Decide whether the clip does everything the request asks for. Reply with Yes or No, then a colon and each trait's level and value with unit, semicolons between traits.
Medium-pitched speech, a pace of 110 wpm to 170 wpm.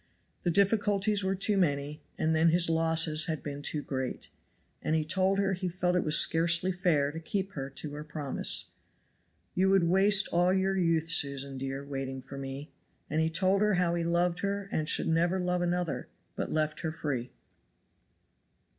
No: medium, 165 Hz; average, 180 wpm